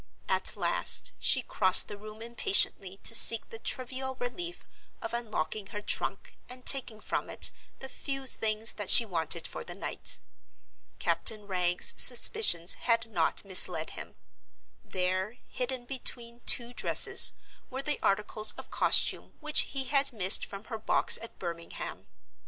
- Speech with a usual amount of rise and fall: Yes, average, 4.4 semitones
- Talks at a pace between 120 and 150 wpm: Yes, average, 145 wpm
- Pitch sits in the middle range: No, high, 225 Hz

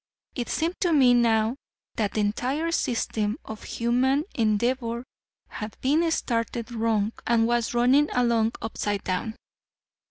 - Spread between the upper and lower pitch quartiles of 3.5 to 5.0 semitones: No, average, 2.7 semitones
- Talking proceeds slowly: Yes, slow, 130 wpm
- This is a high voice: Yes, high, 235 Hz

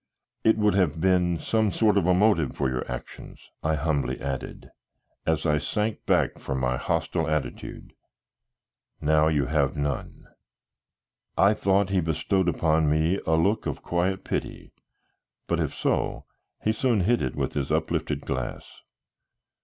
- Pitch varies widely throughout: No, average, 4.7 semitones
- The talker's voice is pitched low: Yes, very low, 80 Hz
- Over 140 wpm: Yes, average, 150 wpm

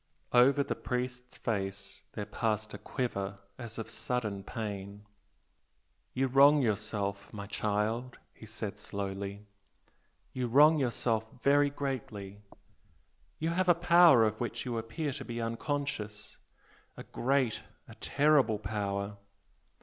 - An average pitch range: Yes, average, 4.5 semitones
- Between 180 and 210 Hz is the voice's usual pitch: No, low, 115 Hz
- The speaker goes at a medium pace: No, slow, 125 wpm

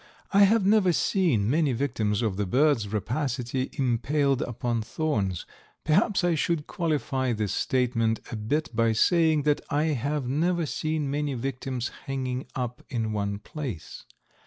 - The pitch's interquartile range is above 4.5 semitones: Yes, average, 5.1 semitones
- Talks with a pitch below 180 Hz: Yes, low, 135 Hz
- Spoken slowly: No, average, 145 wpm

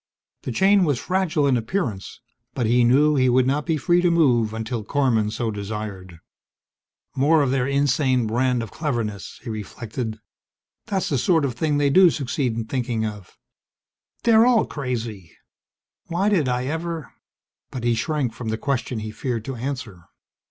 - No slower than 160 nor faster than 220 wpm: Yes, average, 165 wpm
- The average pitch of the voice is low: Yes, low, 130 Hz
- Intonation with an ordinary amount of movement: Yes, average, 4.9 semitones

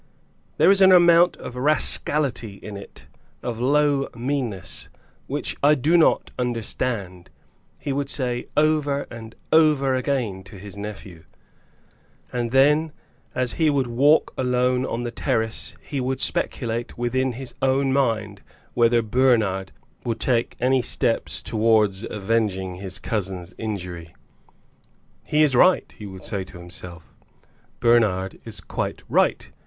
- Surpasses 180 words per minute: No, slow, 135 wpm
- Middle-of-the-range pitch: No, low, 120 Hz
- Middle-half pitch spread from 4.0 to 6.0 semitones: Yes, average, 4.8 semitones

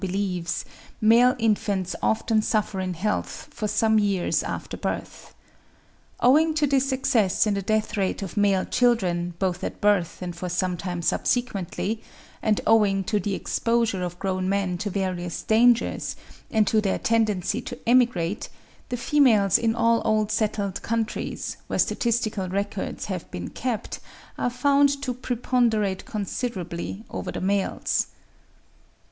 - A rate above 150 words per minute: No, average, 140 wpm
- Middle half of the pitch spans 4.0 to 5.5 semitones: No, average, 3.6 semitones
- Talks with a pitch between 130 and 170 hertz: No, high, 210 Hz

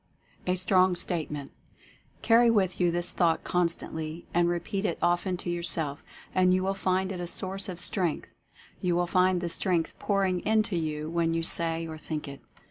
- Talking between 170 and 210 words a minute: Yes, average, 185 wpm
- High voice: No, medium, 175 Hz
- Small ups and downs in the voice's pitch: Yes, narrow, 2.0 semitones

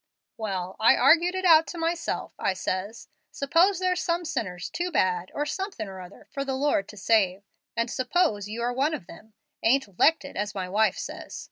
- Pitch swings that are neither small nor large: No, wide, 8.8 semitones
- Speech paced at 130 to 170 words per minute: No, average, 200 wpm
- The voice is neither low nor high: No, high, 240 Hz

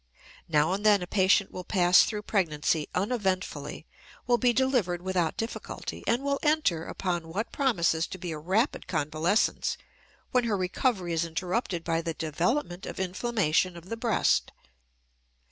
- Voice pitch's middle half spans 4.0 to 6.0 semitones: Yes, average, 5.2 semitones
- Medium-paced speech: Yes, average, 150 wpm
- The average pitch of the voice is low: No, medium, 185 Hz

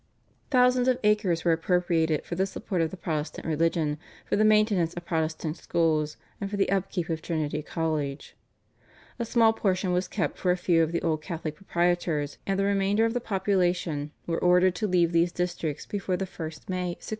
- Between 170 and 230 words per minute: Yes, average, 190 wpm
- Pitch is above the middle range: No, medium, 175 Hz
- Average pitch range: Yes, average, 3.3 semitones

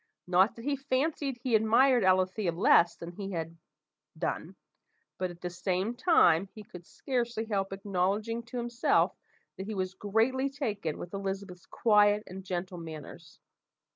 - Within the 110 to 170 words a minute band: Yes, average, 150 wpm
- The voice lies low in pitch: No, high, 200 Hz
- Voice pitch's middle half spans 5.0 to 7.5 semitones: No, average, 4.5 semitones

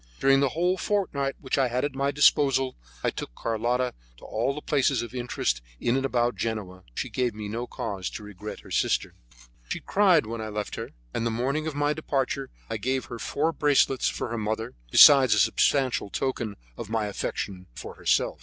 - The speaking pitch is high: No, low, 125 Hz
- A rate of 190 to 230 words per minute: Yes, average, 200 wpm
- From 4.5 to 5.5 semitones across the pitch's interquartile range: No, average, 3.9 semitones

